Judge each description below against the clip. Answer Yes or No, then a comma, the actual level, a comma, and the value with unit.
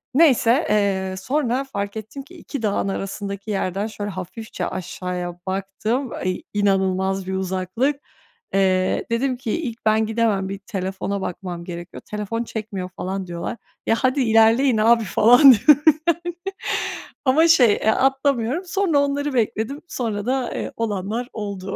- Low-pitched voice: No, high, 215 Hz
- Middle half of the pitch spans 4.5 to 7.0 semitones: Yes, average, 5.0 semitones